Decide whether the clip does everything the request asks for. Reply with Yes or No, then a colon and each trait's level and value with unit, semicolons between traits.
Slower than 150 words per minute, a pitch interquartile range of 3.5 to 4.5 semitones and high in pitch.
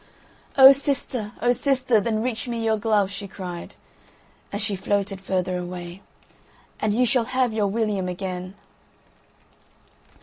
Yes: slow, 135 wpm; average, 3.8 semitones; high, 210 Hz